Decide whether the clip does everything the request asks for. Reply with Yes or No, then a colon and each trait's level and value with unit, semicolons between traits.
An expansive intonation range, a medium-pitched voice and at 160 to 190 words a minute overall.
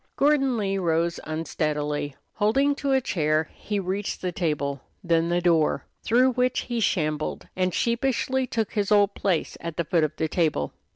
Yes: wide, 6.7 semitones; medium, 180 Hz; average, 170 wpm